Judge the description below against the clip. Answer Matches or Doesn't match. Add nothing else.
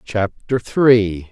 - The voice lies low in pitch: Matches